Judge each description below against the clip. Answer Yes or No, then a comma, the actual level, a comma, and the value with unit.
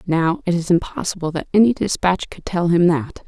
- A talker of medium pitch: Yes, medium, 175 Hz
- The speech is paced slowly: No, average, 200 wpm